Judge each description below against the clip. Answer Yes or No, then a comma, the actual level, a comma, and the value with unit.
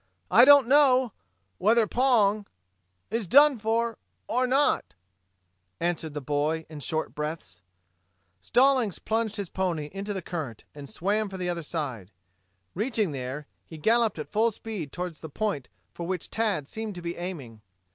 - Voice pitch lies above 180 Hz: Yes, high, 190 Hz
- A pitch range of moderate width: No, wide, 6.5 semitones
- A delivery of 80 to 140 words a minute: No, average, 155 wpm